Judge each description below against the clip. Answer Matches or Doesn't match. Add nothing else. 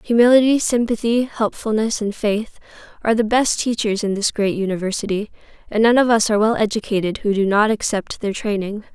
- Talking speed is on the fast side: Doesn't match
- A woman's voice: Matches